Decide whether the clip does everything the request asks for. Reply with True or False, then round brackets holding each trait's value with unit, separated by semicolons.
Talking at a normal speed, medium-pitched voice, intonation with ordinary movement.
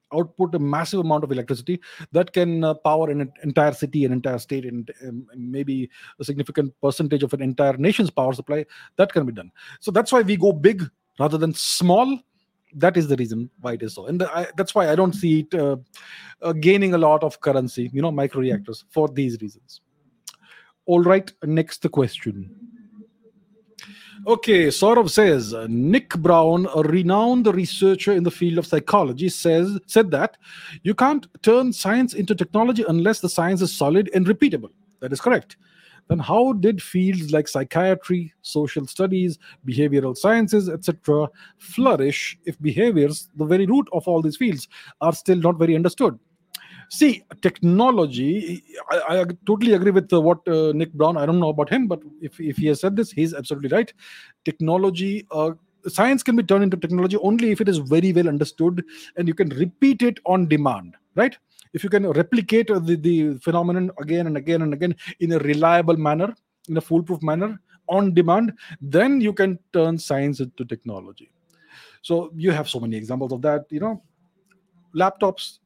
True (175 wpm; 170 Hz; 4.6 semitones)